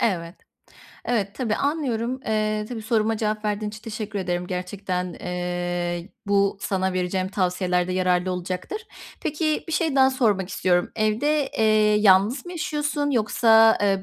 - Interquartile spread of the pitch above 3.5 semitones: Yes, average, 4.2 semitones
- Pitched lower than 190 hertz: No, high, 210 Hz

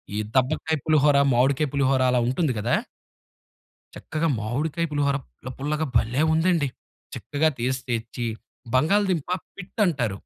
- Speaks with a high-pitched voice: No, medium, 140 Hz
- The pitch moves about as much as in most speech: Yes, average, 3.8 semitones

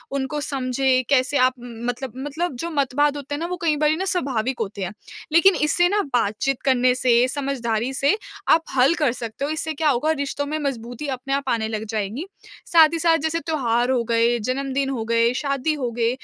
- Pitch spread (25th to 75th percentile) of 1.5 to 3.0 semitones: No, average, 3.8 semitones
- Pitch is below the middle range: No, very high, 270 Hz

